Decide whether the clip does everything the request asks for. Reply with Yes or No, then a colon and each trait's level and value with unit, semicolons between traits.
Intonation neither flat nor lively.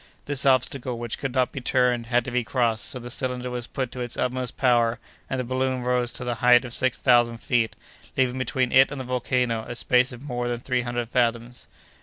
No: narrow, 1.1 semitones